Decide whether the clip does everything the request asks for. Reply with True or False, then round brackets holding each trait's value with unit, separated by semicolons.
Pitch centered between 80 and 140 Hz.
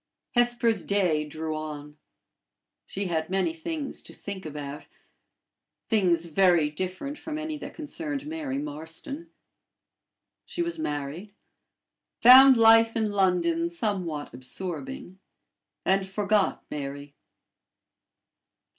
False (190 Hz)